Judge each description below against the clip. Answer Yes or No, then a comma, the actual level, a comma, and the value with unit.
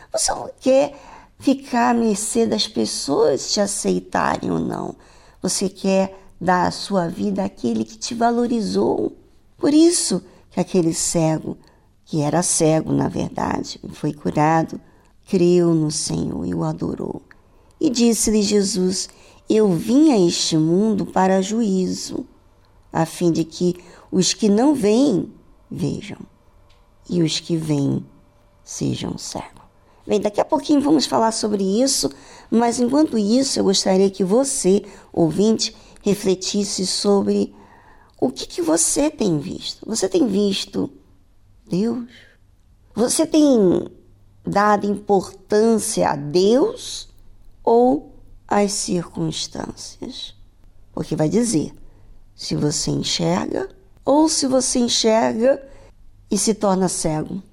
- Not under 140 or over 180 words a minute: No, slow, 120 wpm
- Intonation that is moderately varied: No, wide, 6.3 semitones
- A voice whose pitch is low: No, high, 195 Hz